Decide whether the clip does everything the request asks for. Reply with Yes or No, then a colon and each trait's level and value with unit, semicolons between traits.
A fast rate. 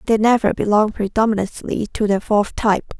No: average, 160 wpm